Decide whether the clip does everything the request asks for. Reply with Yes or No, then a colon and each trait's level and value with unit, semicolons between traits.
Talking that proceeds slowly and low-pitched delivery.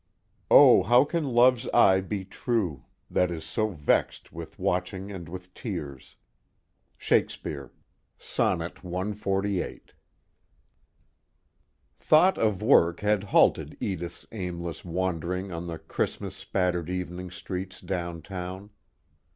Yes: slow, 110 wpm; very low, 90 Hz